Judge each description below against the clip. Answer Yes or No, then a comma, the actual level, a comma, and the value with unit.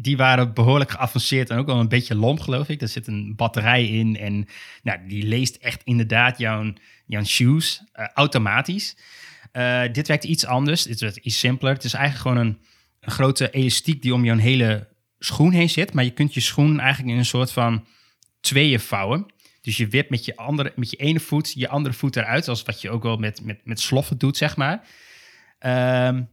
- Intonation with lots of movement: No, average, 3.4 semitones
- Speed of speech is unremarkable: No, fast, 205 wpm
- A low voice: Yes, low, 125 Hz